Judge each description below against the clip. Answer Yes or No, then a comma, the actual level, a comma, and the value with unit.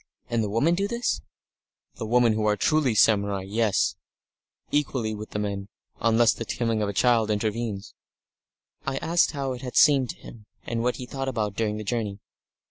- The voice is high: No, low, 115 Hz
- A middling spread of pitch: Yes, average, 3.2 semitones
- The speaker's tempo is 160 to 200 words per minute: Yes, average, 185 wpm